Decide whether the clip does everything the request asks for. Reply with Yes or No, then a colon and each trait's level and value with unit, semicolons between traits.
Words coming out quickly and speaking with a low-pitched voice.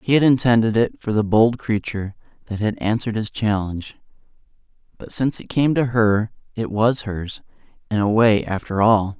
No: average, 175 wpm; low, 110 Hz